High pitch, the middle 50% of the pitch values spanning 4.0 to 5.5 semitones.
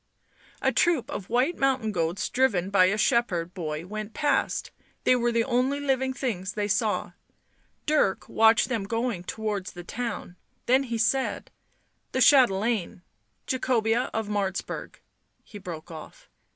Yes: high, 220 Hz; average, 4.8 semitones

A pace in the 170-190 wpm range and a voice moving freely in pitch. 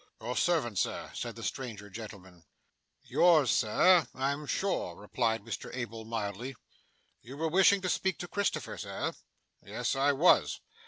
No: average, 145 wpm; wide, 6.8 semitones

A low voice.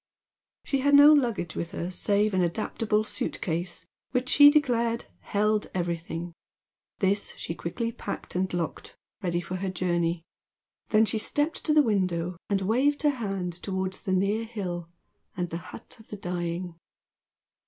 No: high, 195 Hz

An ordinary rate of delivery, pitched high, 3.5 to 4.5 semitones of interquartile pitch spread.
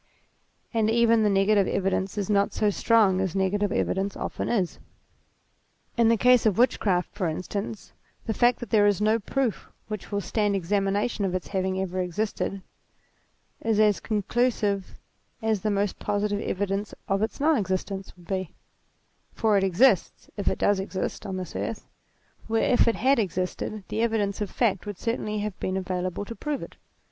No: average, 175 wpm; high, 205 Hz; narrow, 2.5 semitones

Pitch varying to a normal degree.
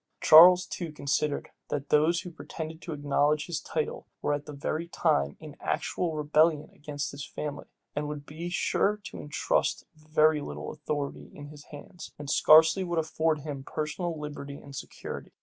No: narrow, 1.7 semitones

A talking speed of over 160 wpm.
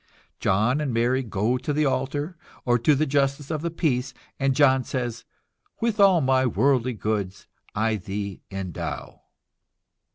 No: average, 150 wpm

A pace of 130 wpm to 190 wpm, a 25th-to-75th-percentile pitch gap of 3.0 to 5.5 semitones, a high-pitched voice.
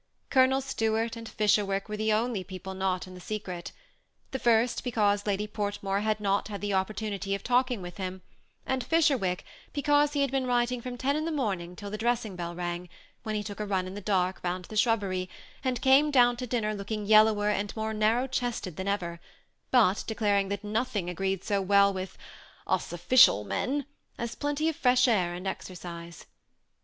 No: average, 200 wpm; average, 4.2 semitones; high, 210 Hz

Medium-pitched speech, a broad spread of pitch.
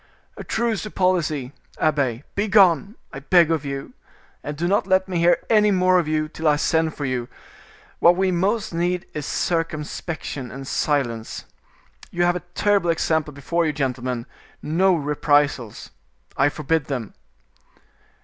No: medium, 160 Hz; average, 4.2 semitones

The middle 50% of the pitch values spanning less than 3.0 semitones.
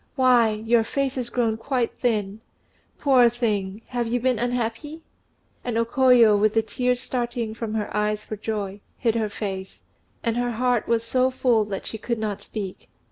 Yes: narrow, 2.4 semitones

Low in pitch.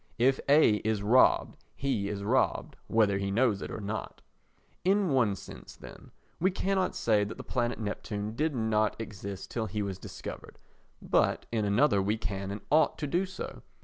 Yes: low, 110 Hz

